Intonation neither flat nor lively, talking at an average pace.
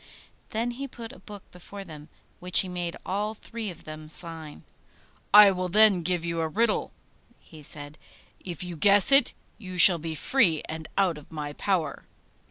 Yes: average, 4.4 semitones; average, 175 wpm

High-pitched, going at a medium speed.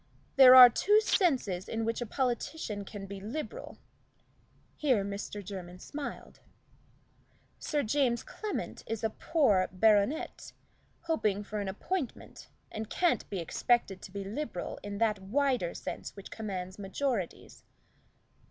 No: high, 220 Hz; slow, 130 wpm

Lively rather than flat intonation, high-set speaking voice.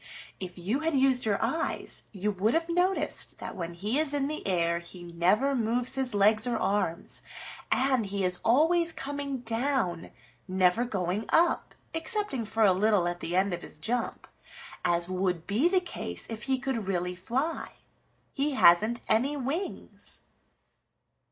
Yes: wide, 6.8 semitones; high, 225 Hz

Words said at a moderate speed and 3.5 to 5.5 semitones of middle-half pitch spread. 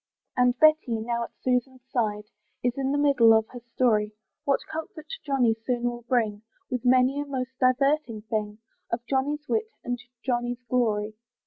No: average, 160 wpm; average, 2.8 semitones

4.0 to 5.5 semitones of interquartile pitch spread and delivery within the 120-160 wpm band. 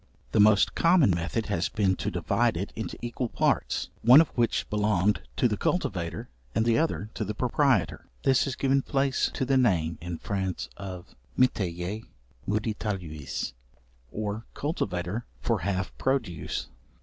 Yes: average, 5.2 semitones; average, 150 wpm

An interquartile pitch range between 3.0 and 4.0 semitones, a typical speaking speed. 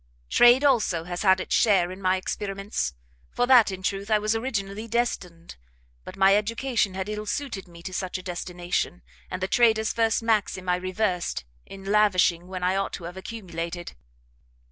Yes: average, 3.3 semitones; average, 175 wpm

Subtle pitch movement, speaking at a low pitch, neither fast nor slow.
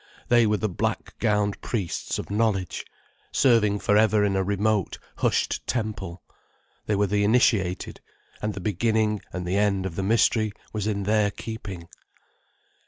Yes: narrow, 2.0 semitones; low, 105 Hz; average, 155 wpm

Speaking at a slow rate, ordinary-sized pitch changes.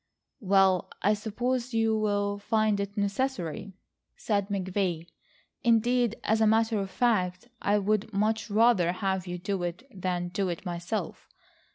No: average, 145 wpm; average, 3.0 semitones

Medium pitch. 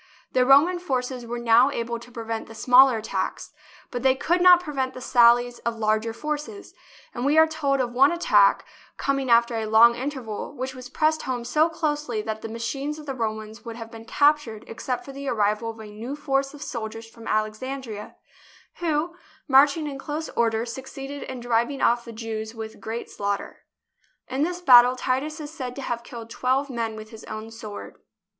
No: high, 245 Hz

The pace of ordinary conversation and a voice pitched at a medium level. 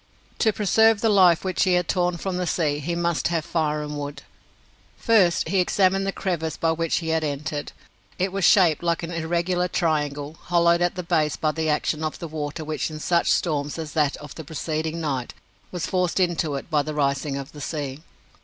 No: fast, 210 wpm; medium, 165 Hz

